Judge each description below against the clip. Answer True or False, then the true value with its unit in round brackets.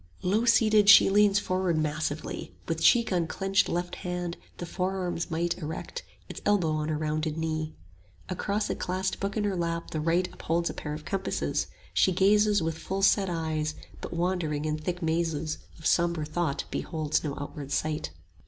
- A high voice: False (170 Hz)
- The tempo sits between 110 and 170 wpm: False (180 wpm)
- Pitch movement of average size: True (3.4 semitones)